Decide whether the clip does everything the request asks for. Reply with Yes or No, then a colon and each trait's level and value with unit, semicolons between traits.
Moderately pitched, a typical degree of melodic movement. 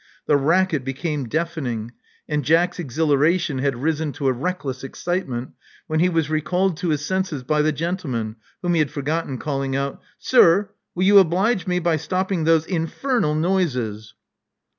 Yes: medium, 155 Hz; average, 4.5 semitones